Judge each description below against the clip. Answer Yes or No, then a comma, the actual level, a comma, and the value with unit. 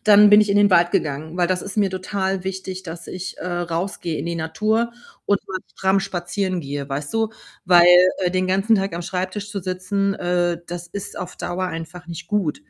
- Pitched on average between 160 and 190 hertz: Yes, medium, 185 Hz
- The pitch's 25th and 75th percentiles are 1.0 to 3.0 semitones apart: Yes, narrow, 2.4 semitones